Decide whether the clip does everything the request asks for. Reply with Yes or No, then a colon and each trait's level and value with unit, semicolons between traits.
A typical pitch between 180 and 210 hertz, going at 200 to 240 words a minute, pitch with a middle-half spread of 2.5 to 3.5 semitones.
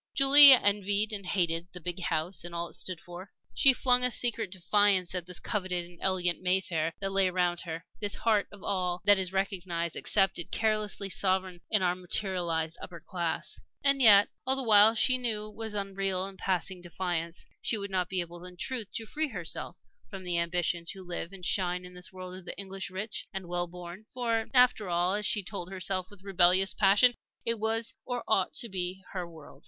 Yes: high, 190 Hz; fast, 205 wpm; average, 2.9 semitones